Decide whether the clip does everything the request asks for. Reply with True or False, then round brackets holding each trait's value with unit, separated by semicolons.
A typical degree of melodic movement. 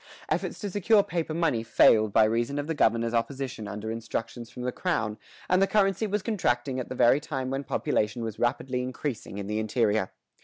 False (6.0 semitones)